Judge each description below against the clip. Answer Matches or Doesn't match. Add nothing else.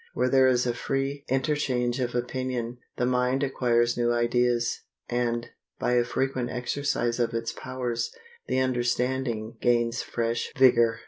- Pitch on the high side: Doesn't match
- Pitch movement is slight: Matches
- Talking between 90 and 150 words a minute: Matches